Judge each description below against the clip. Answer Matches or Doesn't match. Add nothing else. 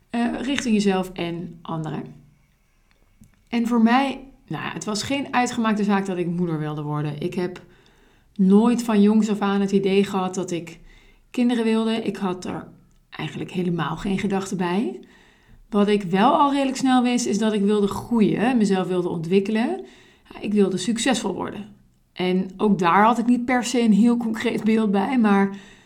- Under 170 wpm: Doesn't match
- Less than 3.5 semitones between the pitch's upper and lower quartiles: Doesn't match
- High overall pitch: Matches